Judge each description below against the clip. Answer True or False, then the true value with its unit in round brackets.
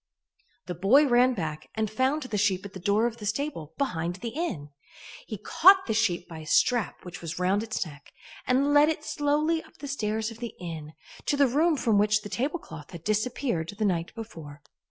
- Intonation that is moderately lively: False (7.3 semitones)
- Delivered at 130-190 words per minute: False (205 wpm)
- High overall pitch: True (215 Hz)